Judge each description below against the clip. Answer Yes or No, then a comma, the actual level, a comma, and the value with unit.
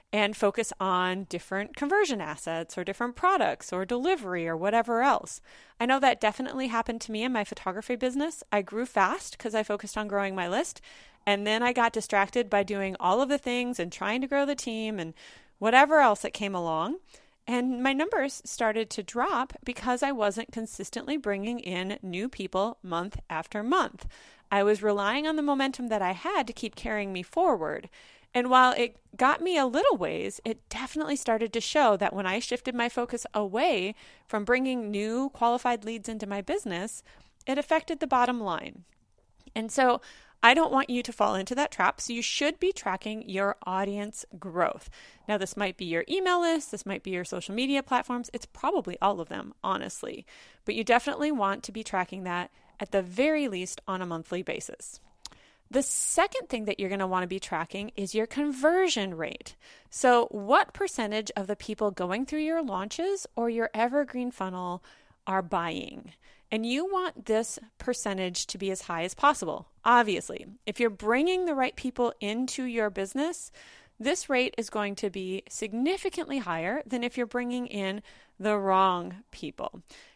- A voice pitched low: No, high, 230 Hz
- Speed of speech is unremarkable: Yes, average, 185 wpm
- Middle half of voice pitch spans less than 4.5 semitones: No, average, 4.8 semitones